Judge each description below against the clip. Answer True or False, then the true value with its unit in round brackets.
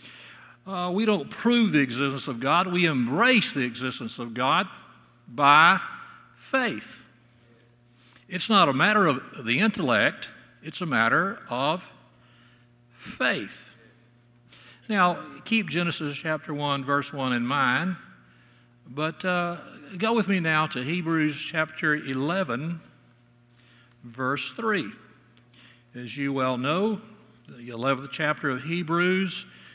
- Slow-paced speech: True (115 wpm)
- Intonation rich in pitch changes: True (6.5 semitones)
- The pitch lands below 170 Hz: True (140 Hz)